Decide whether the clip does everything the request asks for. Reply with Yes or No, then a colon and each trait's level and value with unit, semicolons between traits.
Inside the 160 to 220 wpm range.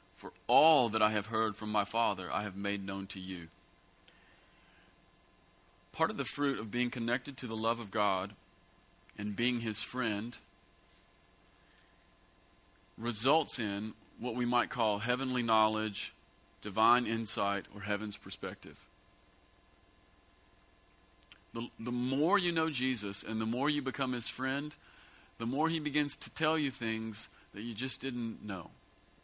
No: average, 145 wpm